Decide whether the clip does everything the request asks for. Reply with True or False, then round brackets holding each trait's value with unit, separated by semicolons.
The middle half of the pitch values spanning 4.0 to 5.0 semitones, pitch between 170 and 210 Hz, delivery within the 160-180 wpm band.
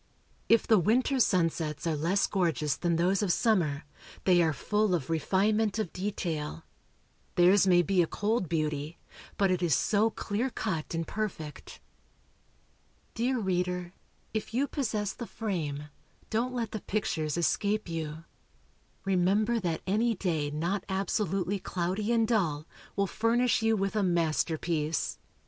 False (4.6 semitones; 185 Hz; 140 wpm)